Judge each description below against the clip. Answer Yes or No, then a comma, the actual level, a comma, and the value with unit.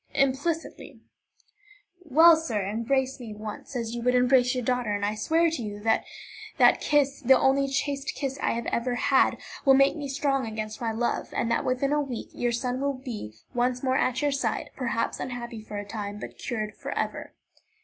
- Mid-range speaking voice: No, very high, 250 Hz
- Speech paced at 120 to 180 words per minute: No, average, 190 wpm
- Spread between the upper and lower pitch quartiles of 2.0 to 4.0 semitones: Yes, average, 3.3 semitones